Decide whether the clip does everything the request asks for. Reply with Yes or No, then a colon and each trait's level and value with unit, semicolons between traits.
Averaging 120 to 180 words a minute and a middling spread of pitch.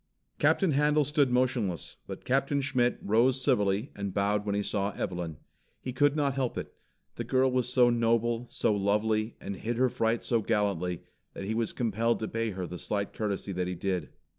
No: average, 190 wpm; average, 4.2 semitones